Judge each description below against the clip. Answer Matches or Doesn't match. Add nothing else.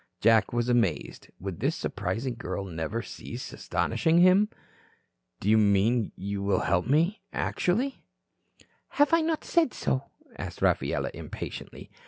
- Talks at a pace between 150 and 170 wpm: Doesn't match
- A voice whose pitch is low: Matches